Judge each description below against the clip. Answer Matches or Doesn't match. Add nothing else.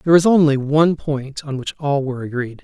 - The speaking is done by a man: Matches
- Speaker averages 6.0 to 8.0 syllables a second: Matches